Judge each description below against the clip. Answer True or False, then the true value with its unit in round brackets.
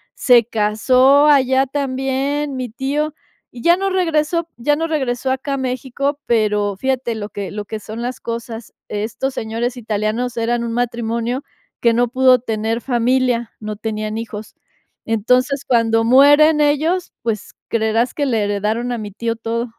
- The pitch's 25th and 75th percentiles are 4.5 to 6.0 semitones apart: False (3.1 semitones)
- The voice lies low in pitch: False (240 Hz)